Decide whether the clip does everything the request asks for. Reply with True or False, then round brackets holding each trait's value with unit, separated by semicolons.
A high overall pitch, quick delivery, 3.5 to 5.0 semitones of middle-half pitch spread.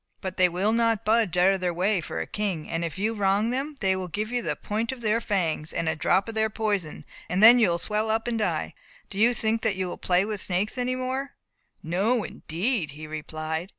True (205 Hz; 240 wpm; 4.1 semitones)